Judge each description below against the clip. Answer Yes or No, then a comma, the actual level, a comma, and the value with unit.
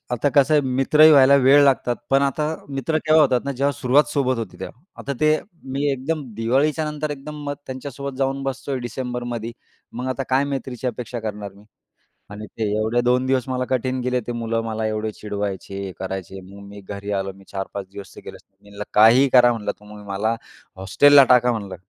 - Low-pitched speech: Yes, low, 125 Hz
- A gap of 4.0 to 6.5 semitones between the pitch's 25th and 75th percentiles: Yes, average, 4.5 semitones